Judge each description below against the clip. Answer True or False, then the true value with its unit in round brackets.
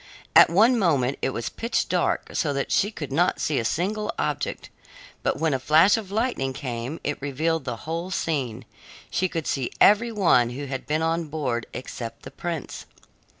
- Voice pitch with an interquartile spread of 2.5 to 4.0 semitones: False (5.4 semitones)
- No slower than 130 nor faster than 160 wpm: False (185 wpm)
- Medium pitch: True (155 Hz)